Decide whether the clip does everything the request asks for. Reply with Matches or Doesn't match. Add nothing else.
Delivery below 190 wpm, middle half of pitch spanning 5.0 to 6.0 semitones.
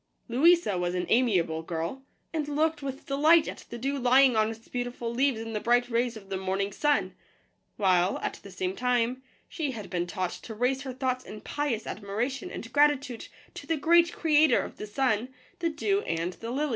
Doesn't match